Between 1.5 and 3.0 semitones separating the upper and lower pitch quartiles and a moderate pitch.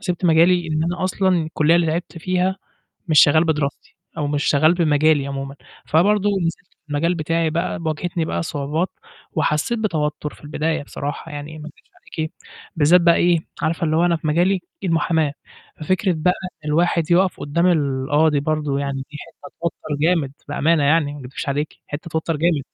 Yes: narrow, 2.6 semitones; medium, 160 Hz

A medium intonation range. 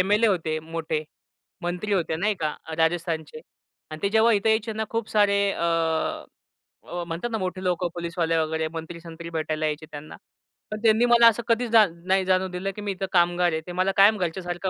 Yes: average, 4.2 semitones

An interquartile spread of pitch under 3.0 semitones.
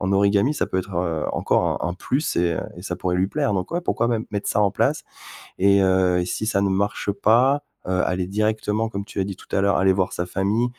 Yes: narrow, 2.6 semitones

